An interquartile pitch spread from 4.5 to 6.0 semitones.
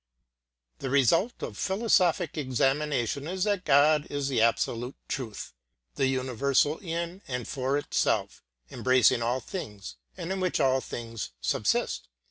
Yes: average, 5.0 semitones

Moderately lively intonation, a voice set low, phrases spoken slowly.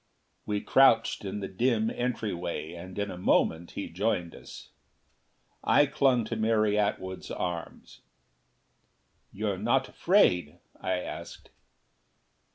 Yes: average, 4.2 semitones; low, 100 Hz; slow, 115 wpm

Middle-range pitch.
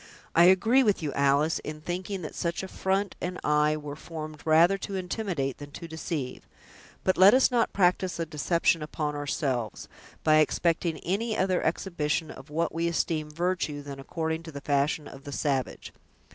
Yes: medium, 160 Hz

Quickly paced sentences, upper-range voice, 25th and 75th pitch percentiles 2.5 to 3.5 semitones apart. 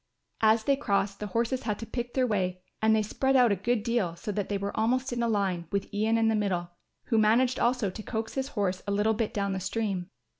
Yes: fast, 250 wpm; high, 215 Hz; average, 3.0 semitones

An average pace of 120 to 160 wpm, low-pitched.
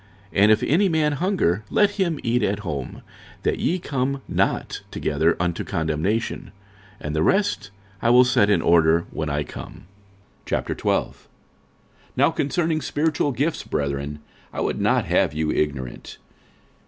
Yes: average, 145 wpm; low, 105 Hz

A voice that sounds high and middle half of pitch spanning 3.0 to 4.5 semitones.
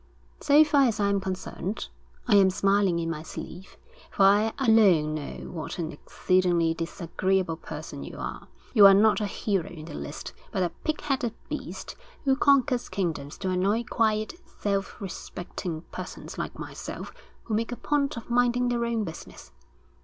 No: high, 200 Hz; average, 4.9 semitones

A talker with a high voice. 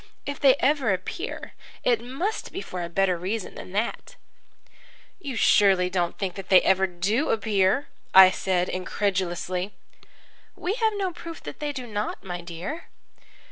Yes: high, 200 Hz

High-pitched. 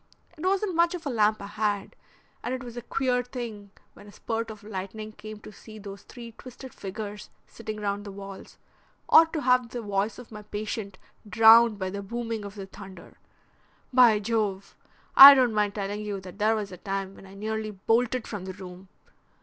Yes: high, 215 Hz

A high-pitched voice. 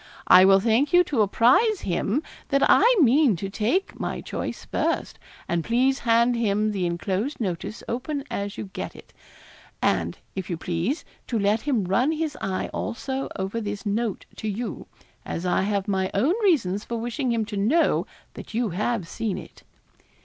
Yes: high, 220 Hz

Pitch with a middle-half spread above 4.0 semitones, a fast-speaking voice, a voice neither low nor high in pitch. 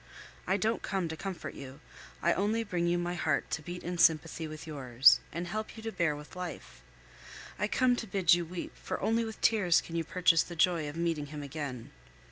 No: average, 3.7 semitones; fast, 215 wpm; medium, 170 Hz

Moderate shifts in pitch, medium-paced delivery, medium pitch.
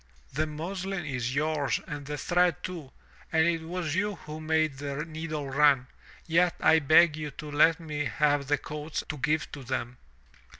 No: narrow, 2.0 semitones; average, 170 wpm; medium, 155 Hz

